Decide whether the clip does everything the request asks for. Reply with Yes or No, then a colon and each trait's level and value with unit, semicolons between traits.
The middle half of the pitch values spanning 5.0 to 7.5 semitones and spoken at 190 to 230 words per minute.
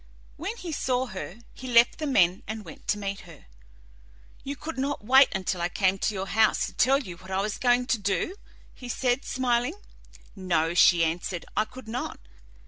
Yes: wide, 5.6 semitones; average, 195 wpm